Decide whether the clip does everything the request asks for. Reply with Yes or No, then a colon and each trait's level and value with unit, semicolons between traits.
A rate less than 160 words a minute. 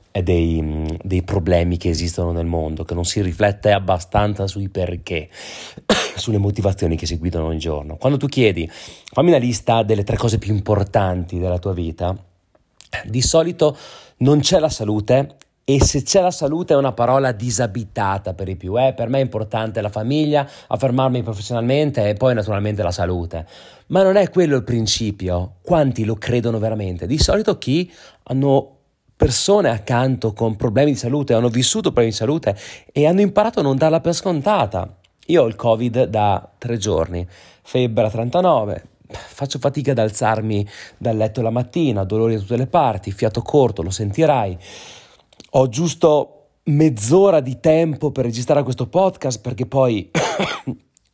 No: average, 165 wpm